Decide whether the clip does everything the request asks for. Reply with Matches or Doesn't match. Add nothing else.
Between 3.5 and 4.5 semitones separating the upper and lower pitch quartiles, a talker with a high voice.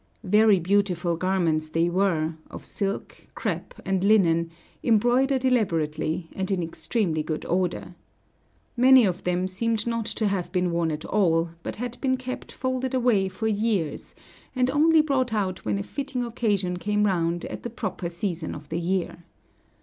Doesn't match